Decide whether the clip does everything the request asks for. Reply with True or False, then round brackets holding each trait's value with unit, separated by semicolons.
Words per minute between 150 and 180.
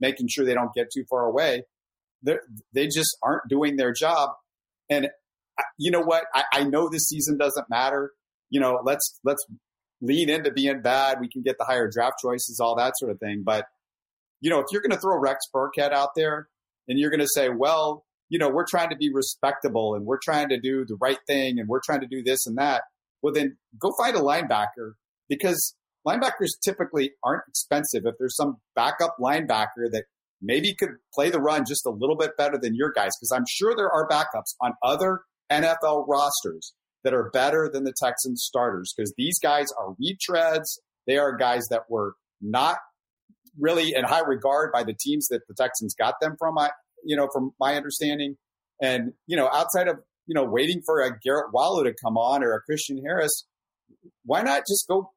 False (205 wpm)